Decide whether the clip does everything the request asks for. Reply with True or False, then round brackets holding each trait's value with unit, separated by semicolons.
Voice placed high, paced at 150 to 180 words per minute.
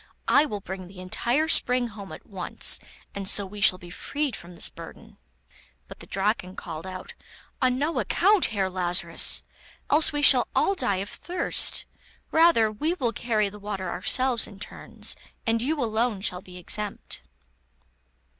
True (210 Hz; 165 wpm)